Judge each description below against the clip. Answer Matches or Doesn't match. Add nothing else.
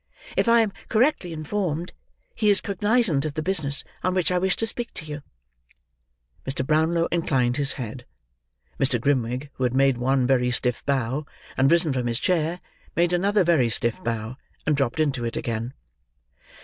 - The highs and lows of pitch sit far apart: Matches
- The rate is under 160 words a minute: Doesn't match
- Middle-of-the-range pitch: Matches